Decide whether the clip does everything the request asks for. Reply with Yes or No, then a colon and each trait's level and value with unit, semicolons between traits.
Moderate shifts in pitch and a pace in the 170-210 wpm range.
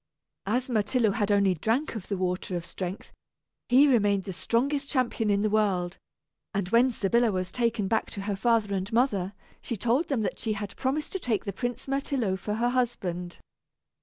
Yes: average, 4.0 semitones; average, 190 wpm